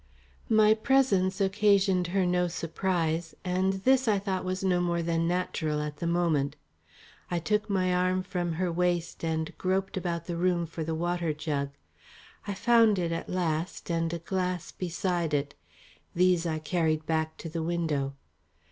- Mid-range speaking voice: Yes, medium, 175 Hz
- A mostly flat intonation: Yes, narrow, 2.3 semitones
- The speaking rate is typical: Yes, average, 165 wpm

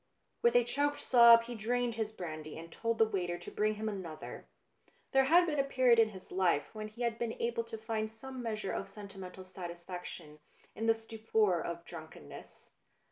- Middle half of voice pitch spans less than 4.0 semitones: No, average, 4.3 semitones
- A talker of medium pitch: No, high, 220 Hz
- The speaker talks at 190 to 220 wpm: Yes, average, 195 wpm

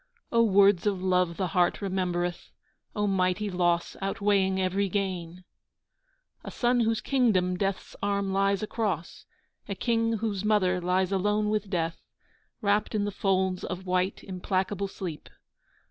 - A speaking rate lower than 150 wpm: Yes, average, 140 wpm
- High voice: Yes, high, 195 Hz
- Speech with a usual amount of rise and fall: No, narrow, 2.2 semitones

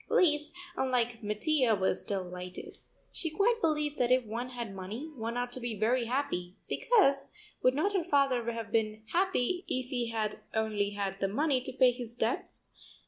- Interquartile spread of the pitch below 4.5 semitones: No, average, 4.8 semitones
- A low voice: No, high, 245 Hz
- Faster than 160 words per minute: Yes, average, 175 wpm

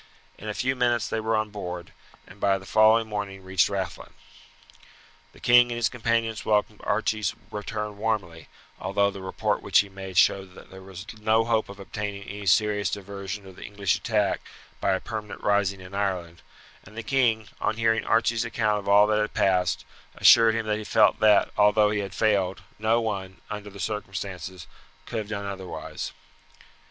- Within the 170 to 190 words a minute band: Yes, average, 185 wpm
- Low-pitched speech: Yes, low, 105 Hz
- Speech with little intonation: Yes, narrow, 2.2 semitones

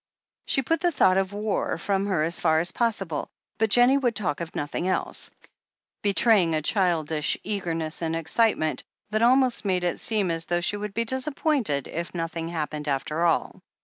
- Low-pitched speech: No, medium, 185 Hz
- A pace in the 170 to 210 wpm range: Yes, average, 180 wpm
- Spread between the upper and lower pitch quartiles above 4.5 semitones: Yes, average, 5.2 semitones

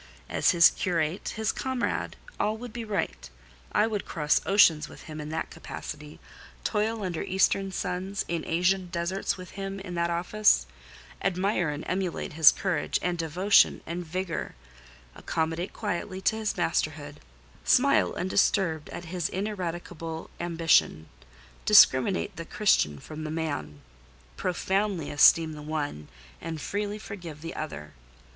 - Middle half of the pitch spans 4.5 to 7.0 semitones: No, average, 3.6 semitones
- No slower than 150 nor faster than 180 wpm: No, average, 140 wpm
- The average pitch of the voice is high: No, medium, 175 Hz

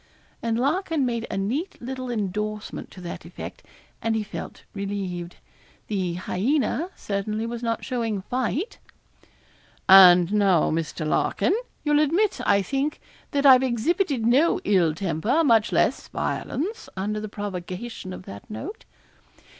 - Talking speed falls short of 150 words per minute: Yes, slow, 135 wpm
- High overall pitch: Yes, high, 220 Hz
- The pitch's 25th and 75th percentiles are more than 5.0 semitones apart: Yes, wide, 5.5 semitones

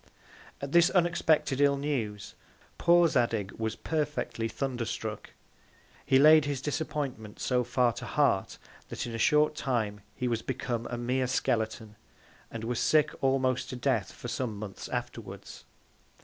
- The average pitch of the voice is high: No, low, 125 Hz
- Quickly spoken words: No, average, 150 wpm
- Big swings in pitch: No, average, 4.1 semitones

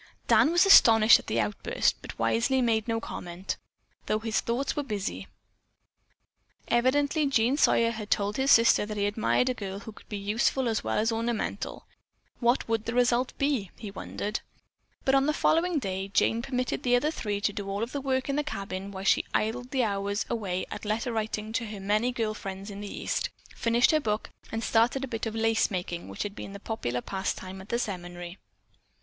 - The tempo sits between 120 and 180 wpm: No, average, 200 wpm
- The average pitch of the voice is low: No, high, 225 Hz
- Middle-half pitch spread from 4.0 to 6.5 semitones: No, average, 3.5 semitones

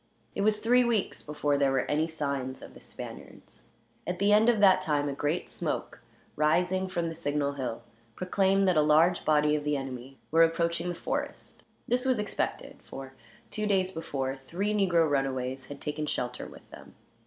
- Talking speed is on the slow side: No, average, 185 wpm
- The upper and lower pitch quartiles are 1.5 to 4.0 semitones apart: No, average, 5.0 semitones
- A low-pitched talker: No, medium, 160 Hz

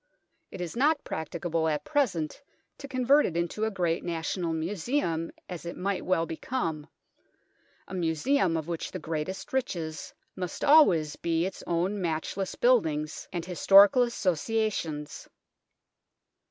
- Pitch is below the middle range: No, medium, 175 Hz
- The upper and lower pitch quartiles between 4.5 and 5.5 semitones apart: Yes, average, 5.0 semitones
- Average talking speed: No, slow, 130 wpm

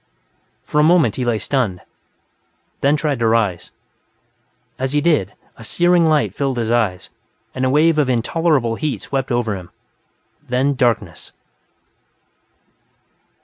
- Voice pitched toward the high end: No, low, 130 Hz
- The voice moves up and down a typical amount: Yes, average, 4.7 semitones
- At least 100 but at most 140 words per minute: Yes, slow, 135 wpm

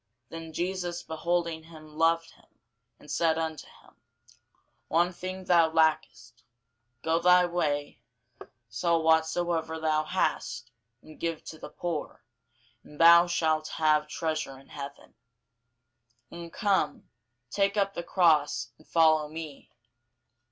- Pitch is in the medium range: Yes, medium, 160 Hz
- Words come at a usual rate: No, slow, 125 wpm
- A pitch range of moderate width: No, narrow, 1.8 semitones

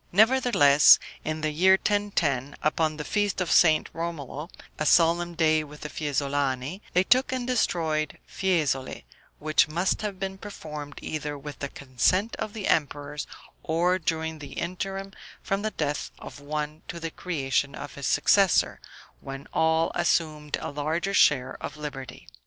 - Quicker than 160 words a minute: No, average, 150 wpm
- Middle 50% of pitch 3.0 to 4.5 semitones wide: Yes, average, 4.0 semitones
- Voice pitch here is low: No, medium, 155 Hz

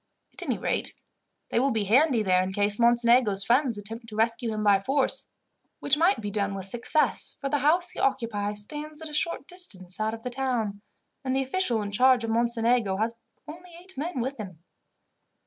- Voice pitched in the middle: No, high, 235 Hz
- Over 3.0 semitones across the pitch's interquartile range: Yes, average, 4.8 semitones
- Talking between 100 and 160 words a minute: No, average, 200 wpm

